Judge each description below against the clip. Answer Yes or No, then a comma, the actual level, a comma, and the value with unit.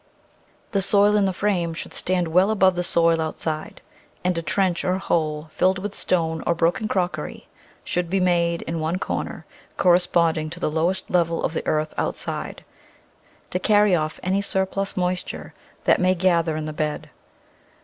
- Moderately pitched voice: Yes, medium, 175 Hz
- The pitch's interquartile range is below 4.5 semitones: Yes, narrow, 2.4 semitones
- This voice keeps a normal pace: Yes, average, 170 wpm